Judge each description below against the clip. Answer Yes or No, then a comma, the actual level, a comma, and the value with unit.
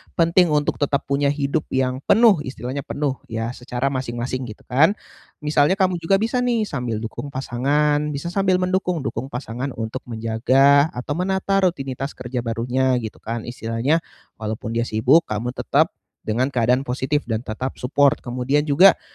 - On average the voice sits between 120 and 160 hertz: Yes, low, 135 Hz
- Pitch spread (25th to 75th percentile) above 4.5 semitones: No, average, 3.8 semitones